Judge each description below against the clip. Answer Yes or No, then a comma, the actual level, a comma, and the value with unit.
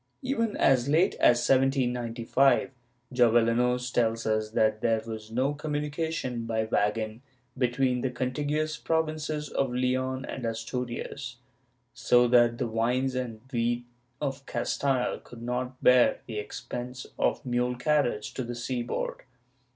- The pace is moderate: No, slow, 130 wpm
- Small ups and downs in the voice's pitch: Yes, narrow, 2.3 semitones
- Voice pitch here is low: Yes, low, 125 Hz